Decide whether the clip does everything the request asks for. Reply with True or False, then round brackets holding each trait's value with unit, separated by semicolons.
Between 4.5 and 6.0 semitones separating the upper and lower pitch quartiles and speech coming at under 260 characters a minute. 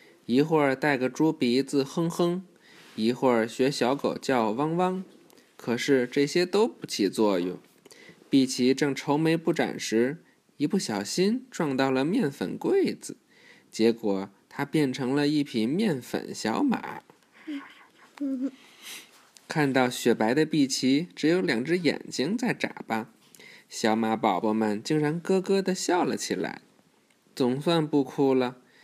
True (5.3 semitones; 195 characters per minute)